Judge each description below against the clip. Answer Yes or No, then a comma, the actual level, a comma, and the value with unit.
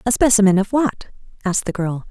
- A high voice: Yes, high, 210 Hz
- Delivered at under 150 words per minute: No, average, 200 wpm